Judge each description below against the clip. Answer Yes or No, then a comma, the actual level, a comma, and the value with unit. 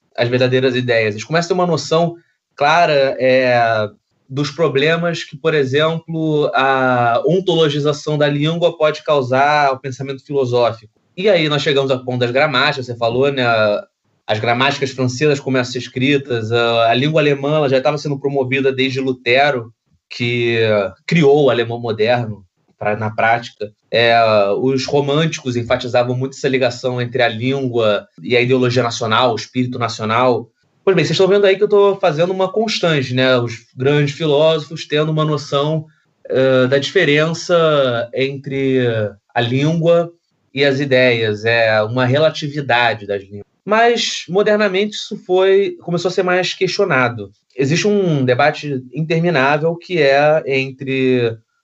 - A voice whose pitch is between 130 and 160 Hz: Yes, low, 135 Hz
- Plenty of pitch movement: No, average, 4.4 semitones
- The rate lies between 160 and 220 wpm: No, average, 145 wpm